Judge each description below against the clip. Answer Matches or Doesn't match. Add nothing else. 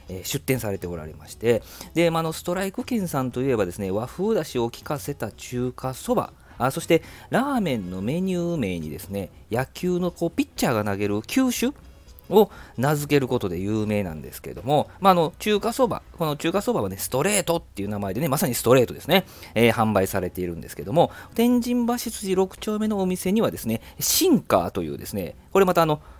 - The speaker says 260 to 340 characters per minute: Doesn't match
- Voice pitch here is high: Doesn't match